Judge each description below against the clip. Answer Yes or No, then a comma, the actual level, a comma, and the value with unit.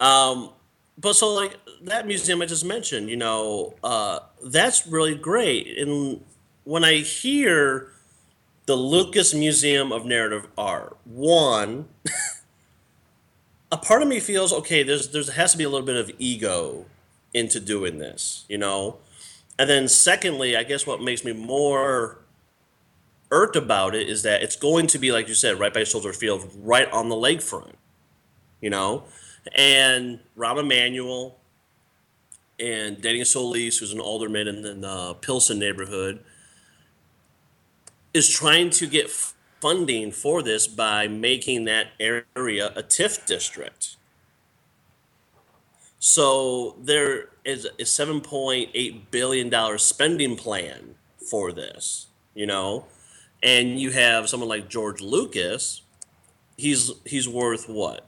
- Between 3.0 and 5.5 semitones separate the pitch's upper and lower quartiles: Yes, average, 5.1 semitones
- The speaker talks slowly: Yes, slow, 130 wpm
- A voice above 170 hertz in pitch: No, low, 130 Hz